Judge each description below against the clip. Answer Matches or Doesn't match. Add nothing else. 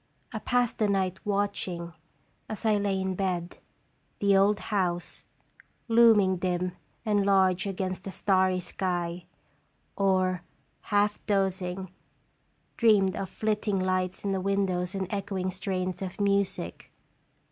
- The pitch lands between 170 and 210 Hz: Matches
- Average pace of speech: Doesn't match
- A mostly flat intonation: Matches